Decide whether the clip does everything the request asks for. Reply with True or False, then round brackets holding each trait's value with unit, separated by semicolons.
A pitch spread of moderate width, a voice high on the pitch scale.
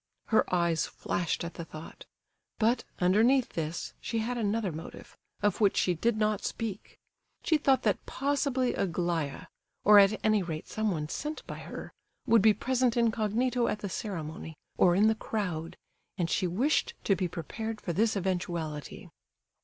True (4.9 semitones; 205 Hz)